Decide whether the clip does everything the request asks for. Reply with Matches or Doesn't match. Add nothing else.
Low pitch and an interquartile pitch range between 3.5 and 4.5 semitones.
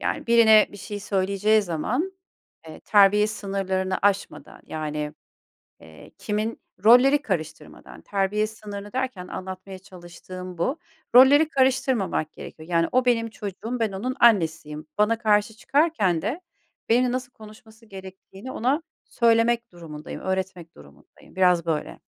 Doesn't match